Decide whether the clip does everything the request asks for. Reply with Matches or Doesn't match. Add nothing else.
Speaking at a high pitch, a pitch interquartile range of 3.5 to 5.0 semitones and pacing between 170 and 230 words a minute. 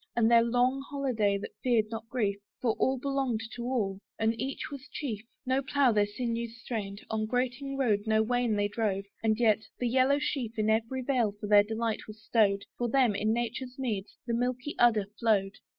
Doesn't match